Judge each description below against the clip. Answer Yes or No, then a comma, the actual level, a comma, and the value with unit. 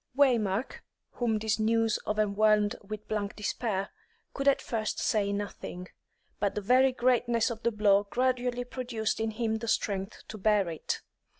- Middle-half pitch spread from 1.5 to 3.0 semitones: Yes, narrow, 2.6 semitones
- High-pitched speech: Yes, high, 220 Hz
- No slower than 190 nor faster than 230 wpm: No, average, 155 wpm